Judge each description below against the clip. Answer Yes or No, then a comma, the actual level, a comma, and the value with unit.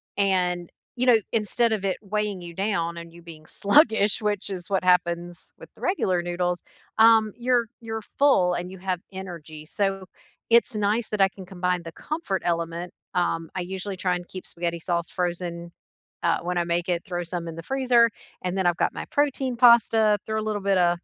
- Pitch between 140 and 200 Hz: Yes, medium, 185 Hz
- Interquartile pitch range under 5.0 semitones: Yes, average, 3.6 semitones